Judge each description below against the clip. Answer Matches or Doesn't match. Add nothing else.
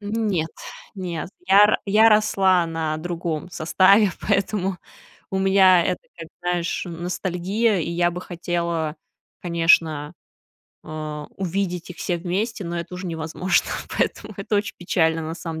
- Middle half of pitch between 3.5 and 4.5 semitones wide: Doesn't match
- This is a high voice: Doesn't match